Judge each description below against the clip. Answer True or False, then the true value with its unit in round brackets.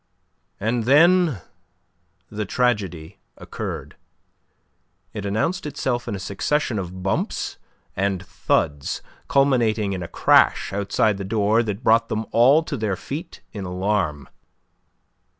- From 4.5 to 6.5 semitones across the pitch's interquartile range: False (4.1 semitones)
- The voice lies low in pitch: True (105 Hz)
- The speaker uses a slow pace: True (120 wpm)